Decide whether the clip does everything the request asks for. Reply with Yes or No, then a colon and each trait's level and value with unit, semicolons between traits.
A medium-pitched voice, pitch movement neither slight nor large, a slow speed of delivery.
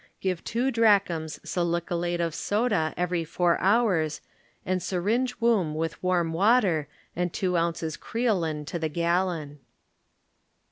Yes: medium, 175 Hz; average, 3.7 semitones; slow, 125 wpm